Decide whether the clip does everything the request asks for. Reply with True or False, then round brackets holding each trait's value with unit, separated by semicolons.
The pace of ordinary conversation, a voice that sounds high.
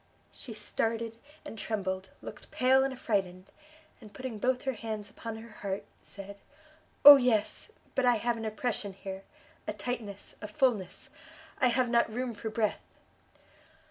True (150 wpm; 225 Hz)